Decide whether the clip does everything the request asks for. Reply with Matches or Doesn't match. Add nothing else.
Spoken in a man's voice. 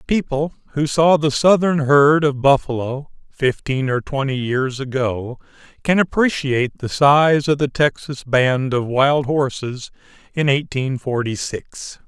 Matches